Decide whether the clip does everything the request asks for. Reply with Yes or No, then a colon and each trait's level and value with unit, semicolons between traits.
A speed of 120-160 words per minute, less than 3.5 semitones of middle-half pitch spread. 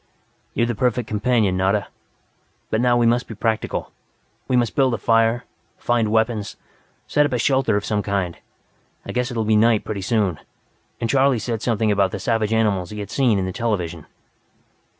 No: average, 185 wpm; average, 2.8 semitones